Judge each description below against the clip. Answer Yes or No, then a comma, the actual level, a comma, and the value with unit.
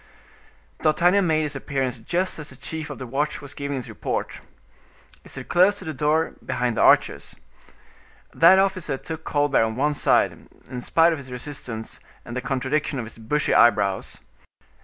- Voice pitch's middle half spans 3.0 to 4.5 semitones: Yes, average, 4.0 semitones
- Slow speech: No, average, 175 wpm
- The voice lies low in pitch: No, medium, 145 Hz